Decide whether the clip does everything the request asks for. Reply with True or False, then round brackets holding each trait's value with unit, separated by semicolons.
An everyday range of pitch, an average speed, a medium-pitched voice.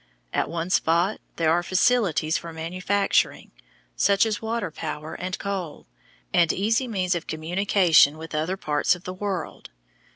True (3.5 semitones; 150 wpm; 180 Hz)